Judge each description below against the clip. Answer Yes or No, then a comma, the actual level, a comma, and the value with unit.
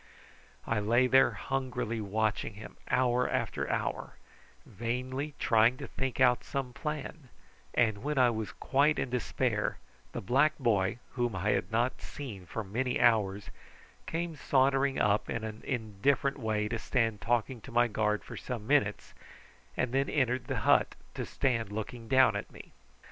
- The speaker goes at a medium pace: Yes, average, 160 wpm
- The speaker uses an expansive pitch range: No, average, 3.3 semitones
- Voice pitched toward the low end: Yes, low, 120 Hz